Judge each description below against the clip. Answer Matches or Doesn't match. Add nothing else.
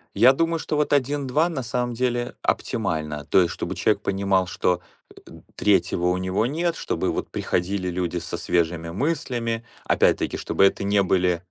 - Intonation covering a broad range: Matches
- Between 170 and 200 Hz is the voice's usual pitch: Doesn't match